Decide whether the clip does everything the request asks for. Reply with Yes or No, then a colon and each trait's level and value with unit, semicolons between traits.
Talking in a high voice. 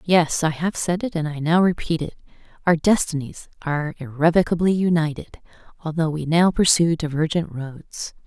No: medium, 165 Hz